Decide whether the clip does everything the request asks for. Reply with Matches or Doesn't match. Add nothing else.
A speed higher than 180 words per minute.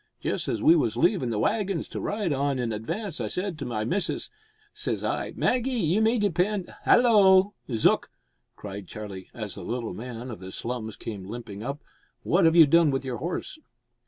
Matches